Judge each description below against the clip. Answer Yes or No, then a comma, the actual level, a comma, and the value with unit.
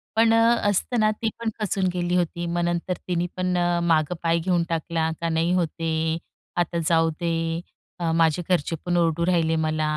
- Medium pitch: Yes, medium, 170 Hz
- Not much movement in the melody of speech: Yes, narrow, 1.7 semitones